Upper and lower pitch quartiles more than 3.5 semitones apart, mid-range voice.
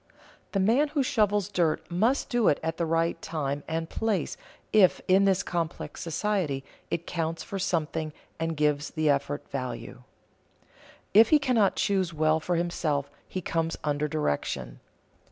Yes: average, 4.5 semitones; medium, 165 Hz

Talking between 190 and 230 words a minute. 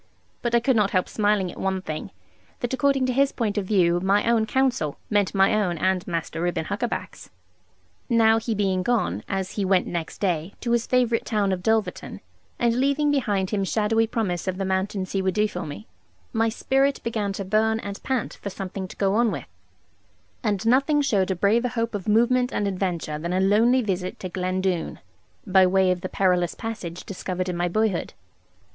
Yes: average, 200 wpm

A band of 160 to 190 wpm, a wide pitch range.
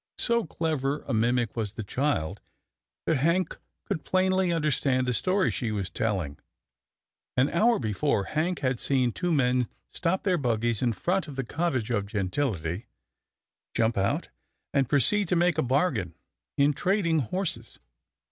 No: average, 150 wpm; wide, 7.0 semitones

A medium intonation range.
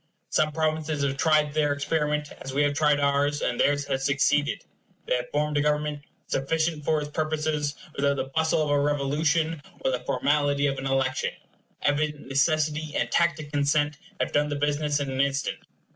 No: narrow, 1.4 semitones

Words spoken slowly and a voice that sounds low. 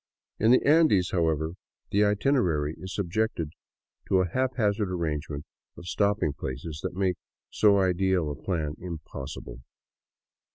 Yes: slow, 130 wpm; very low, 90 Hz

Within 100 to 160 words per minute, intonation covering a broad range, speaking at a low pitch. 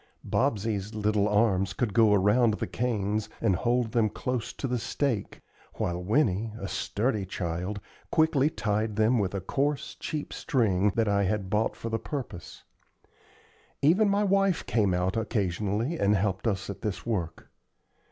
No: average, 155 wpm; average, 3.8 semitones; low, 110 Hz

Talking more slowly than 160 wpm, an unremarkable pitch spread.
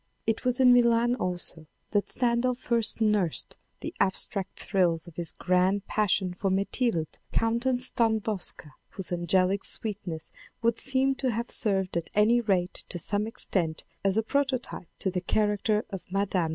Yes: average, 150 wpm; average, 4.3 semitones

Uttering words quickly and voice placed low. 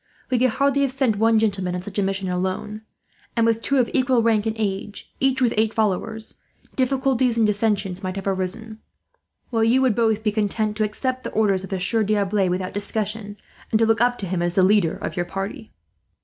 No: fast, 215 wpm; high, 215 Hz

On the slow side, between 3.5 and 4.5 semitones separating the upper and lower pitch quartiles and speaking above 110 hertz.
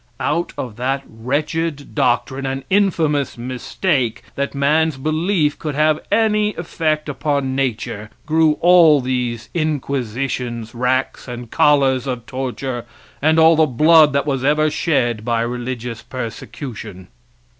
Yes: slow, 125 wpm; average, 4.0 semitones; low, 135 Hz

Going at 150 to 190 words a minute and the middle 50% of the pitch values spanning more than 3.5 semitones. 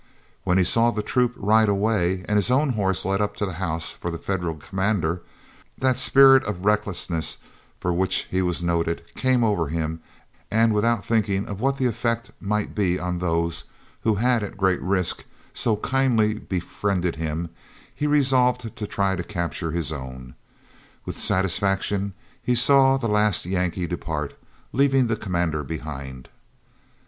Yes: average, 160 wpm; average, 4.6 semitones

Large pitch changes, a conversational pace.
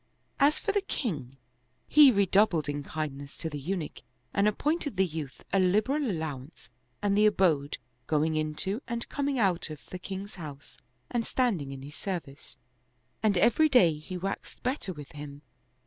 Yes: wide, 6.4 semitones; average, 165 wpm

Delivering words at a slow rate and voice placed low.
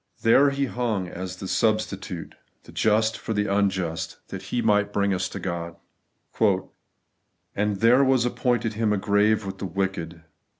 No: average, 170 wpm; low, 105 Hz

